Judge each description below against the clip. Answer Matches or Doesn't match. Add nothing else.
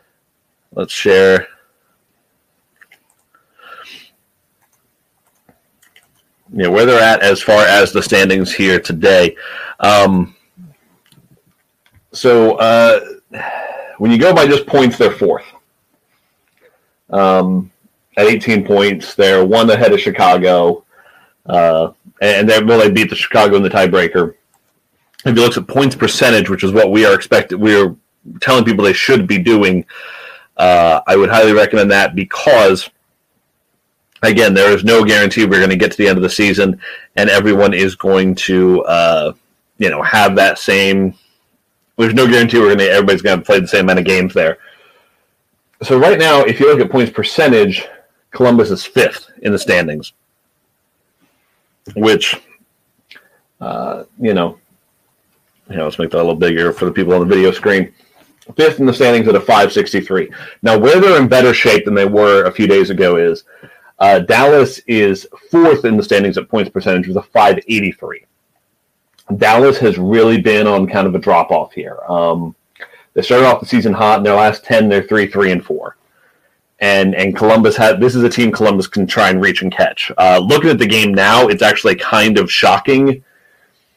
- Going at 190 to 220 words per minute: Doesn't match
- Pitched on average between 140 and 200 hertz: Doesn't match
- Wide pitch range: Doesn't match